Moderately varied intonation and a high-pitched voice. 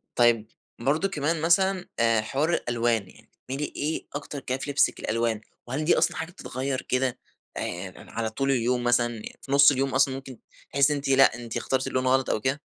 No: average, 3.1 semitones; low, 130 Hz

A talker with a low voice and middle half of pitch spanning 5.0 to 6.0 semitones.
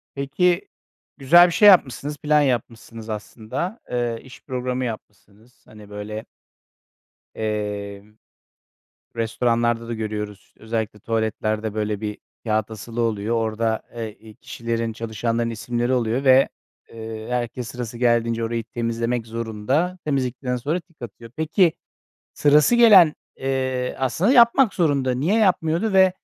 No: low, 120 Hz; average, 3.9 semitones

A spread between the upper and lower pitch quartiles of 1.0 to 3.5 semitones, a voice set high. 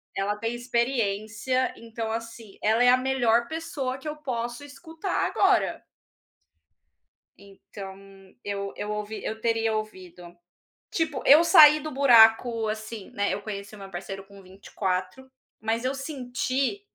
No: average, 4.4 semitones; high, 230 Hz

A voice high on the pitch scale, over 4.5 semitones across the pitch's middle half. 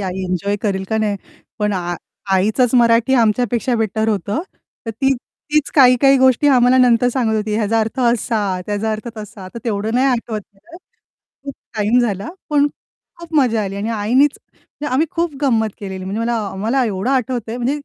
No: high, 225 Hz; average, 3.6 semitones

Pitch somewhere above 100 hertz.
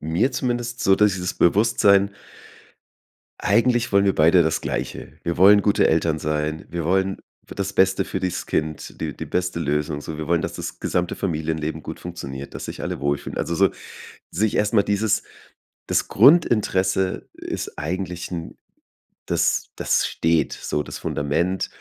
No: very low, 90 Hz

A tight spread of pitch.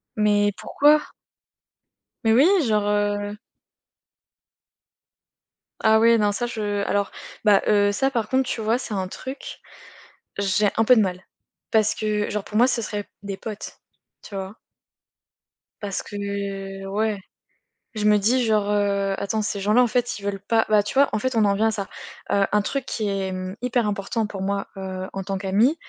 Yes: narrow, 1.9 semitones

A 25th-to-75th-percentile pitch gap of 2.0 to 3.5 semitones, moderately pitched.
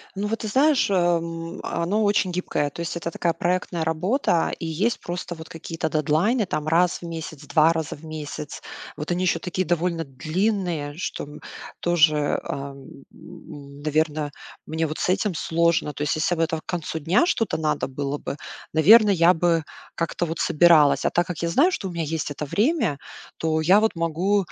Yes: average, 2.7 semitones; medium, 165 Hz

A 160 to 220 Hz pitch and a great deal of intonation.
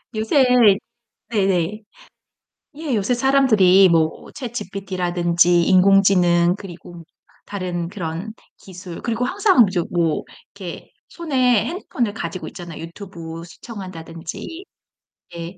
No: high, 190 Hz; average, 4.4 semitones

